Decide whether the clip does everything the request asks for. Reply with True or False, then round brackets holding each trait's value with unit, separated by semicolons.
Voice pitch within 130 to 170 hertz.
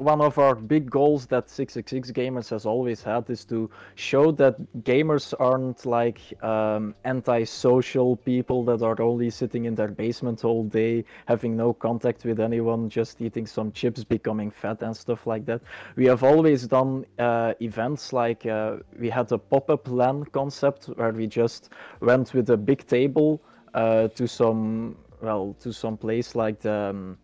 False (120 Hz)